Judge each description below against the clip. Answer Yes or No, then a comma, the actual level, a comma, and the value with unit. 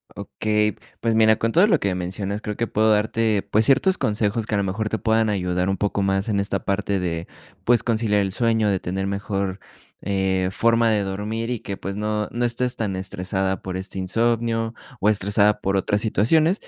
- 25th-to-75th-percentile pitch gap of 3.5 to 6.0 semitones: No, average, 2.7 semitones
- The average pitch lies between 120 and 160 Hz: No, low, 105 Hz